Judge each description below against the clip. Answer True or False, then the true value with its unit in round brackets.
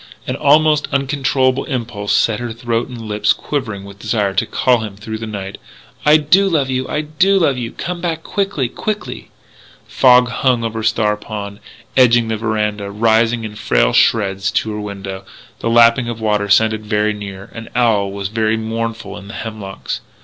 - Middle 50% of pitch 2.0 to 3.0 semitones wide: False (3.5 semitones)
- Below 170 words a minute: False (185 wpm)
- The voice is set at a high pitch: False (115 Hz)